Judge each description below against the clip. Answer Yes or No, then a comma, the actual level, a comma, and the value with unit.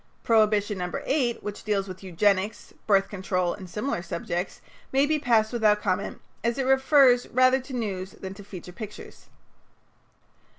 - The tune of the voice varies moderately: Yes, average, 4.5 semitones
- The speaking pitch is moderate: No, high, 210 Hz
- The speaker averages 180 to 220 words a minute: No, average, 155 wpm